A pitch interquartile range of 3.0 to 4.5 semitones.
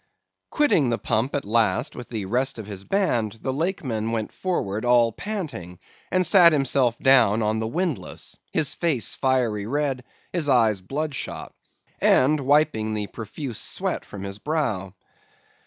No: wide, 5.5 semitones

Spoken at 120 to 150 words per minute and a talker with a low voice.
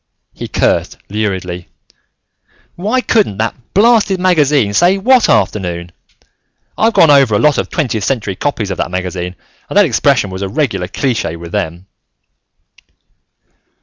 Yes: average, 140 wpm; low, 115 Hz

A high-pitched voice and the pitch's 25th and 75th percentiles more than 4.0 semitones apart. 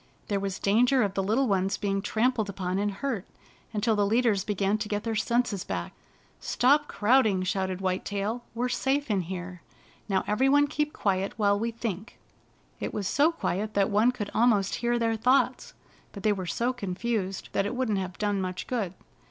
No: high, 210 Hz; average, 3.6 semitones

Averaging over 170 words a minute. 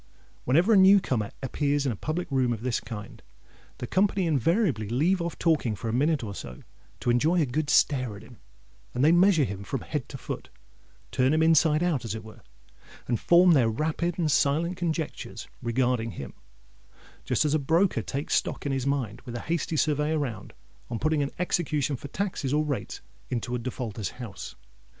Yes: average, 185 wpm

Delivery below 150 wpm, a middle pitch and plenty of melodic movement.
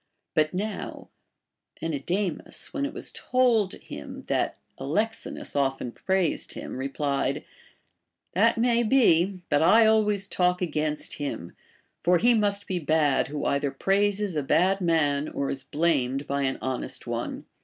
Yes: average, 140 wpm; medium, 170 Hz; wide, 6.3 semitones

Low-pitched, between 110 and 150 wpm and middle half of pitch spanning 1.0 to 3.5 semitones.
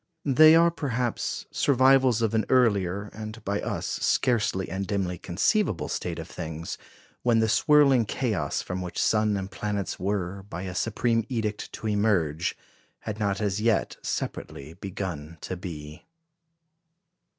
No: low, 105 Hz; average, 140 wpm; average, 4.0 semitones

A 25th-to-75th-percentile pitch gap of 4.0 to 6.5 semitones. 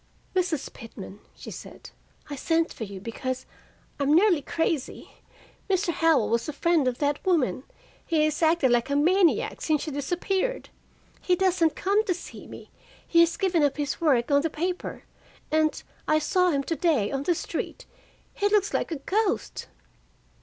Yes: average, 4.3 semitones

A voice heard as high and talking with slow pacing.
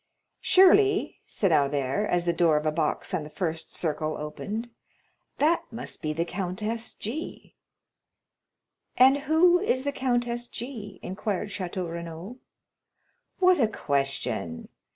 Yes: high, 200 Hz; slow, 130 wpm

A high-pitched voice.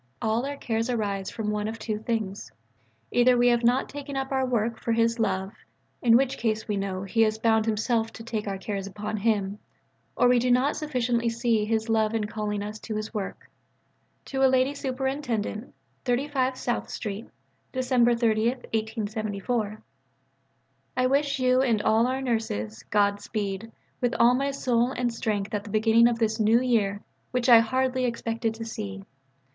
Yes: high, 230 Hz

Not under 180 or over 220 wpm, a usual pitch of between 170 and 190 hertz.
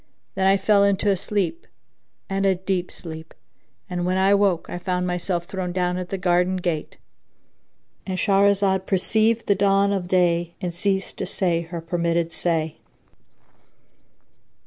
No: average, 145 wpm; medium, 185 Hz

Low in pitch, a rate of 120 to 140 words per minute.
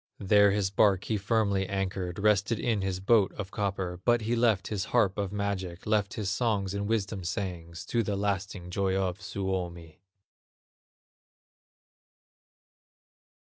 Yes: low, 100 Hz; slow, 135 wpm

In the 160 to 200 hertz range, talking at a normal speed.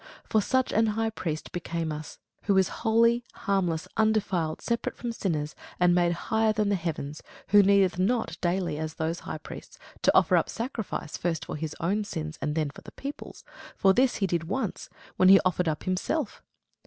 Yes: medium, 185 Hz; average, 190 wpm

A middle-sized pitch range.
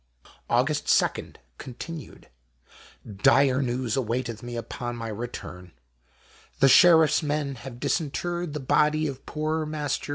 Yes: average, 4.1 semitones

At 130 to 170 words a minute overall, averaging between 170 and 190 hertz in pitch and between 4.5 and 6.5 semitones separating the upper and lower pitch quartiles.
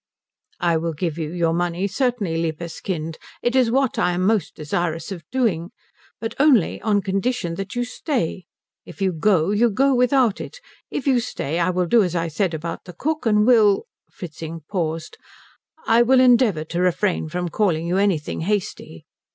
No: average, 185 wpm; medium, 185 Hz; wide, 5.5 semitones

